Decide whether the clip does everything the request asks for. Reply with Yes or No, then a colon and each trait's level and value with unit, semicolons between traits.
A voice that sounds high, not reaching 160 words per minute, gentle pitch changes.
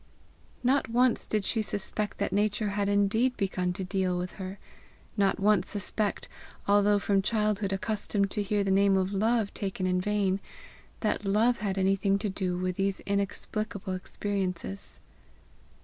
Yes: high, 200 Hz; average, 150 wpm; narrow, 1.6 semitones